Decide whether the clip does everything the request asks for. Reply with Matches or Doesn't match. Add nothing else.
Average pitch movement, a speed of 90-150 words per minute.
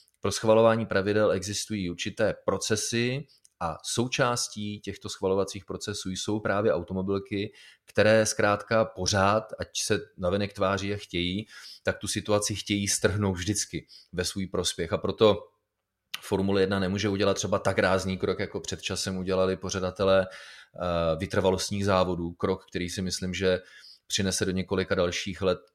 Doesn't match